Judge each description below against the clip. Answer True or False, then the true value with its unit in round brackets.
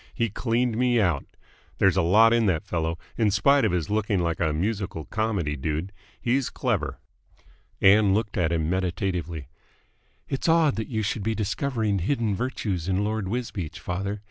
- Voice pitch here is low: True (100 Hz)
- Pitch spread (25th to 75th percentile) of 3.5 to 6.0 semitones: True (4.4 semitones)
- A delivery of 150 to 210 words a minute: True (170 wpm)